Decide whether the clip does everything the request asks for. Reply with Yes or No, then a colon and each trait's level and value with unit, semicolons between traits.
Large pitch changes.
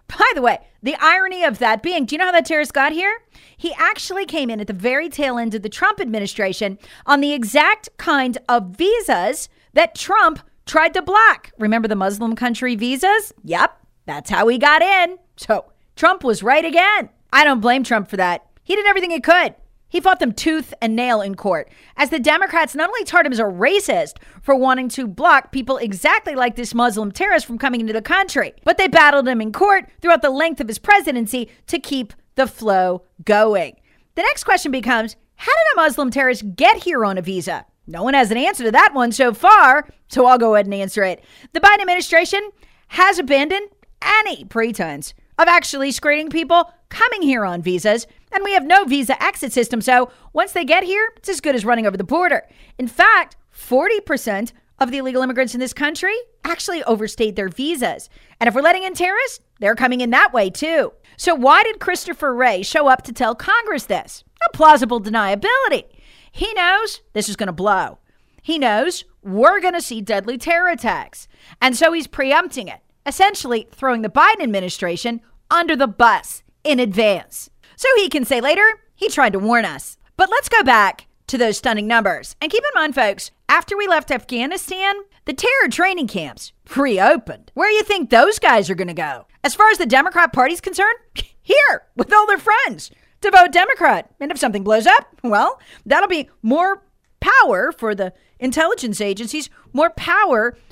Yes: wide, 7.4 semitones